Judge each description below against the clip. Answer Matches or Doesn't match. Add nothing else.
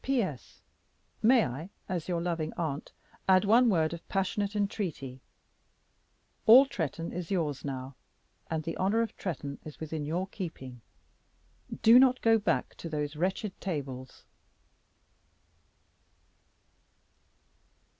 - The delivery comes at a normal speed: Doesn't match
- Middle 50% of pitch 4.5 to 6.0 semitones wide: Matches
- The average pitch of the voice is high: Doesn't match